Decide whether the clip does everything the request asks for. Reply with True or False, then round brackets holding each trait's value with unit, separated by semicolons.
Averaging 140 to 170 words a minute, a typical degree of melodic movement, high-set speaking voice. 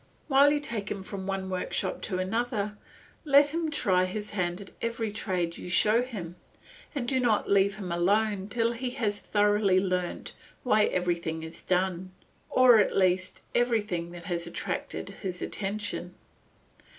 True (160 wpm; 3.9 semitones; 200 Hz)